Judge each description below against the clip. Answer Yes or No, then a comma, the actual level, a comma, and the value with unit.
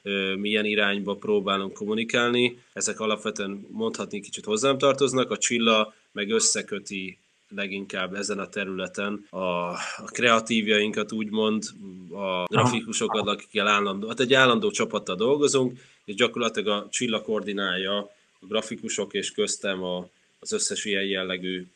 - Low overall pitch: Yes, low, 105 Hz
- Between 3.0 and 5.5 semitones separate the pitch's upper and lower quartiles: No, narrow, 2.4 semitones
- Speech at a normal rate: Yes, average, 120 wpm